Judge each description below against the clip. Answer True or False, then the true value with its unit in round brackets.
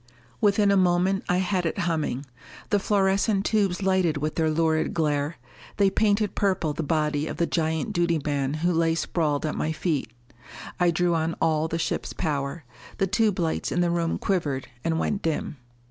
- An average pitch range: True (3.4 semitones)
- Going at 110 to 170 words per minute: False (180 wpm)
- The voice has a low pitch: False (165 Hz)